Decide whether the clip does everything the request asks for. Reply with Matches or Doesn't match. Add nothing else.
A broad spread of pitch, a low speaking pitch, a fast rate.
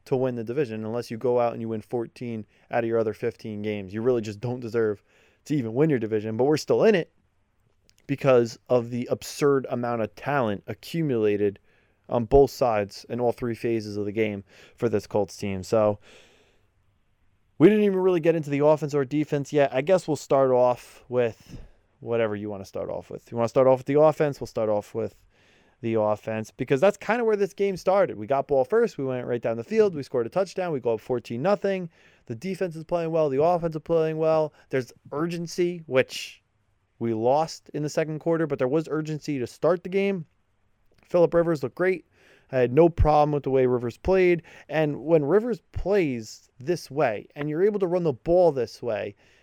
Matches